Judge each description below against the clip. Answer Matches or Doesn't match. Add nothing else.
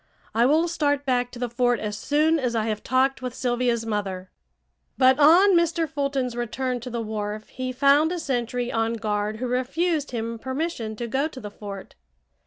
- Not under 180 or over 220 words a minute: Matches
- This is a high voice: Matches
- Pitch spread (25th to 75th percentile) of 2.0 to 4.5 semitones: Matches